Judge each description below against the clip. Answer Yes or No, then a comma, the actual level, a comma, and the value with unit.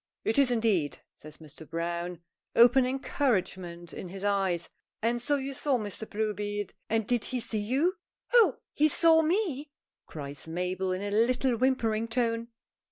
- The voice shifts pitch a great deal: Yes, wide, 5.8 semitones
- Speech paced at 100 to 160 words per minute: Yes, average, 155 wpm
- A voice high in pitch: Yes, high, 225 Hz